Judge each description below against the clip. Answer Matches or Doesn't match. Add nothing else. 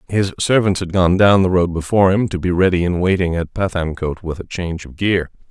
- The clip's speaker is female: Doesn't match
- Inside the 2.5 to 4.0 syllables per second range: Doesn't match